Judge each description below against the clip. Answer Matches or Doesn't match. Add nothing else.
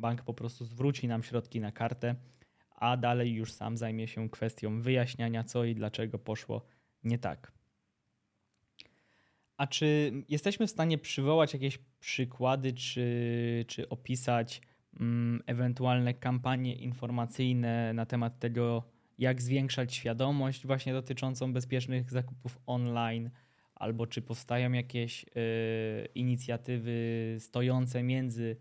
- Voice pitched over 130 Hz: Doesn't match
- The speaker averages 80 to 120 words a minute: Matches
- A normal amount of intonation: Doesn't match